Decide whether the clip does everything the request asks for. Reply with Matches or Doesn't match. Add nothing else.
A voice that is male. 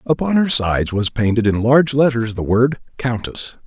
Matches